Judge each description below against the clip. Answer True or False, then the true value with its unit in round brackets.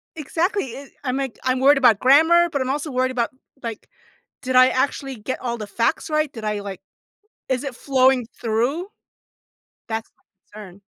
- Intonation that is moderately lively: True (3.5 semitones)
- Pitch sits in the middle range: False (255 Hz)